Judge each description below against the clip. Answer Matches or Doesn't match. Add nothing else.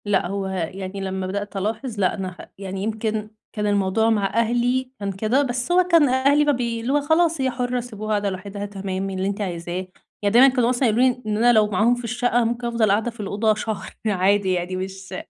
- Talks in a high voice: Matches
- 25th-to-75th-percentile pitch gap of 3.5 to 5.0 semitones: Matches